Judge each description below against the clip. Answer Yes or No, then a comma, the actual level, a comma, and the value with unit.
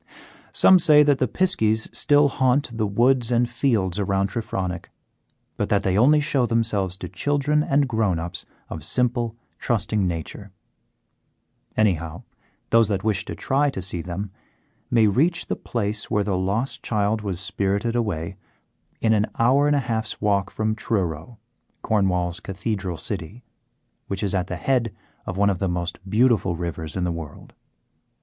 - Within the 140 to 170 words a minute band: Yes, average, 160 wpm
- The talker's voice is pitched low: Yes, low, 105 Hz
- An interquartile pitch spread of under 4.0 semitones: No, average, 4.4 semitones